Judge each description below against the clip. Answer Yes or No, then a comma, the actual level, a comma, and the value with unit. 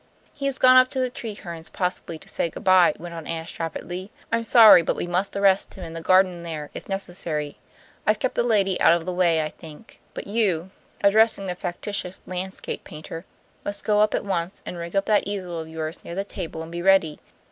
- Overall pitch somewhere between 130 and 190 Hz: Yes, medium, 185 Hz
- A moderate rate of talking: No, fast, 220 wpm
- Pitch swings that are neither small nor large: Yes, average, 3.3 semitones